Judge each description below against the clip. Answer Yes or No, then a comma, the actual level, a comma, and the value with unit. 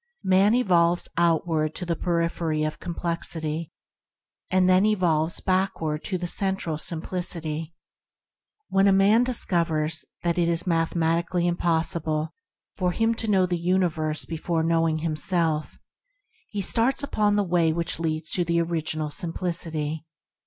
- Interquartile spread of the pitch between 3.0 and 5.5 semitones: No, narrow, 2.4 semitones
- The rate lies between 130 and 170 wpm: Yes, average, 140 wpm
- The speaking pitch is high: No, medium, 170 Hz